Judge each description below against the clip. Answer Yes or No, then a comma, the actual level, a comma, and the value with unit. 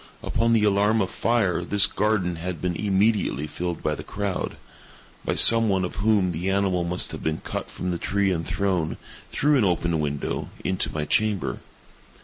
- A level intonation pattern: No, average, 3.2 semitones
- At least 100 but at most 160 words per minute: No, average, 175 wpm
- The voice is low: Yes, very low, 95 Hz